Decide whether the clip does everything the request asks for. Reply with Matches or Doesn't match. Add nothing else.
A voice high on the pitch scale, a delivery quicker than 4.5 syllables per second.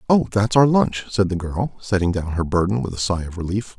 Doesn't match